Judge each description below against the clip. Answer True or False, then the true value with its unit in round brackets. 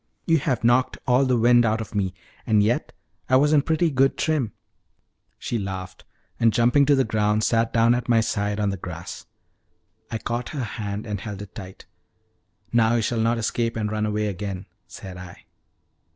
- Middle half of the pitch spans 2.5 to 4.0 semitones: True (2.9 semitones)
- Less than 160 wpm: False (190 wpm)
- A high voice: False (115 Hz)